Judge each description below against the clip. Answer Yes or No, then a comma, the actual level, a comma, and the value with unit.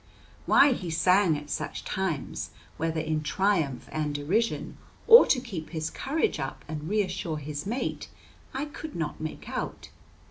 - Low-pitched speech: No, medium, 165 Hz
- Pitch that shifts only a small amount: No, average, 5.3 semitones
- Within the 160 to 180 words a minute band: No, average, 150 wpm